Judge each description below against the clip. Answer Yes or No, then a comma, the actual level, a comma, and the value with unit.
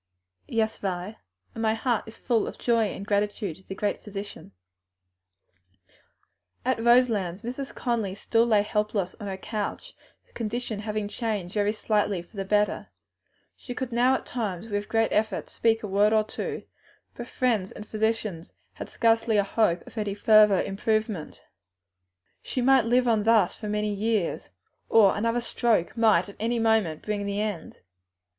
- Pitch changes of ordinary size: No, narrow, 2.1 semitones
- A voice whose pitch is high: Yes, high, 215 Hz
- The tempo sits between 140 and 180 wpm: Yes, average, 160 wpm